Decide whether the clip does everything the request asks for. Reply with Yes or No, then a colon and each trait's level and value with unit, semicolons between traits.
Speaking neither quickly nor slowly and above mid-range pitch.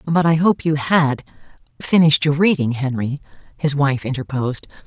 No: average, 150 wpm; medium, 145 Hz